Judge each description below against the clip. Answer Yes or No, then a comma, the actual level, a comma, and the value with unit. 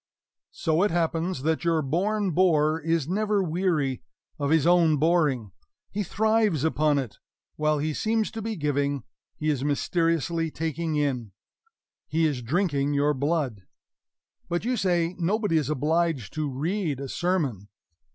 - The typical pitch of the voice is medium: Yes, medium, 160 Hz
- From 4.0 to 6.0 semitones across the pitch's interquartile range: No, average, 3.6 semitones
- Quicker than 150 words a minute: No, average, 145 wpm